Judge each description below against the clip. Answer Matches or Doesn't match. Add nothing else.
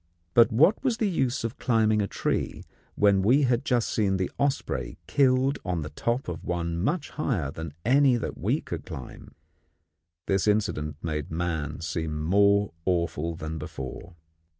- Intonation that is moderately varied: Doesn't match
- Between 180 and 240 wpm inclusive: Doesn't match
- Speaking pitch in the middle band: Doesn't match